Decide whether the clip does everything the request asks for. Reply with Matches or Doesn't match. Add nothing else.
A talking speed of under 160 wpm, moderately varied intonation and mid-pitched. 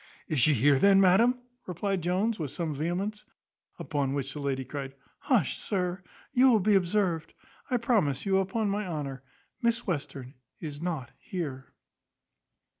Doesn't match